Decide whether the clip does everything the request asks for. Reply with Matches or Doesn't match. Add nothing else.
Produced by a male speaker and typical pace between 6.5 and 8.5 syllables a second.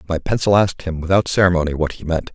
Matches